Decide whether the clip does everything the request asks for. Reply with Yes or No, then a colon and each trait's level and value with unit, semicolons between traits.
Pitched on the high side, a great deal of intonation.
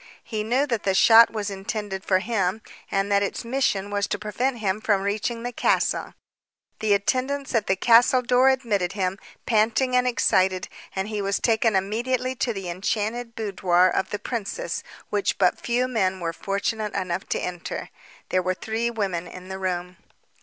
No: high, 210 Hz; average, 3.5 semitones